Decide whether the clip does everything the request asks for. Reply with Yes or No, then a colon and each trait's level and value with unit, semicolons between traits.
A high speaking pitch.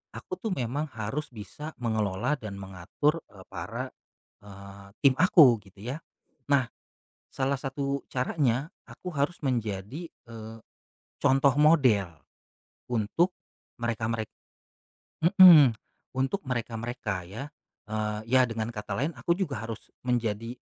No: low, 120 Hz